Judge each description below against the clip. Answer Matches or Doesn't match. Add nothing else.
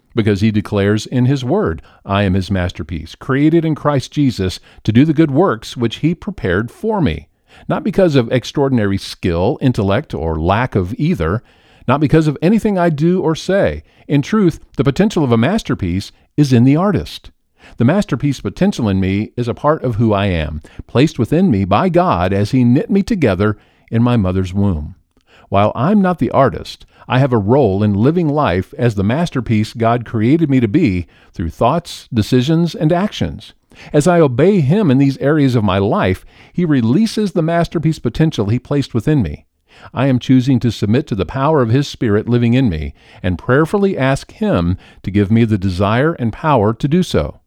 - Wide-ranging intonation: Matches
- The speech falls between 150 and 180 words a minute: Doesn't match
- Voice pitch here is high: Doesn't match